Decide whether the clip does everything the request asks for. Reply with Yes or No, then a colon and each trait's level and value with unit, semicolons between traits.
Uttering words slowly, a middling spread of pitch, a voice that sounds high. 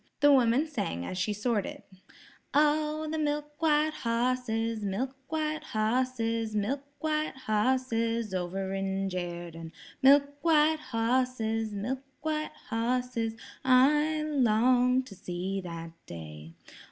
No: slow, 115 wpm; wide, 5.7 semitones; high, 245 Hz